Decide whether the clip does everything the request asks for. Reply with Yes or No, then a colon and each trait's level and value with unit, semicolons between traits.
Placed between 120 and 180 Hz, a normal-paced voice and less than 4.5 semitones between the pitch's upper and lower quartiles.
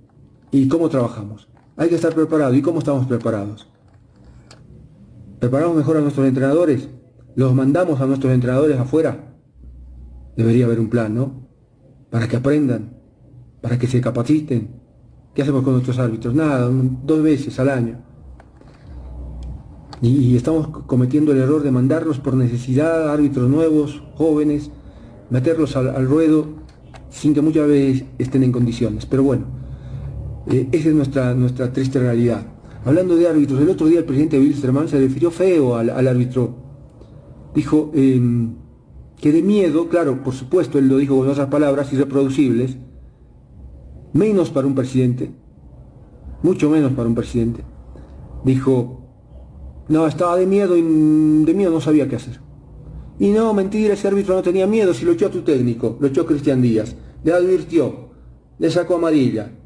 Yes: low, 135 Hz; average, 150 wpm; average, 3.9 semitones